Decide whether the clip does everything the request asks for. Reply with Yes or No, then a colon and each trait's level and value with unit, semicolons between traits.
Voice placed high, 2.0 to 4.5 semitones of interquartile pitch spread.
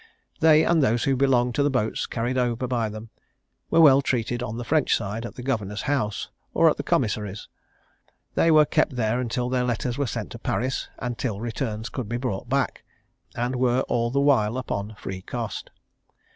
No: low, 120 Hz; average, 3.1 semitones